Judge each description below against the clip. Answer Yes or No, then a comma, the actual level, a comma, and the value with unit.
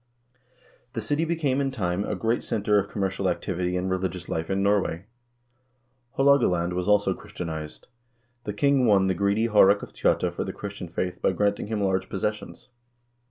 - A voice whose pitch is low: Yes, low, 100 Hz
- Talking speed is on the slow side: No, average, 170 wpm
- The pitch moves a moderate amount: Yes, average, 4.5 semitones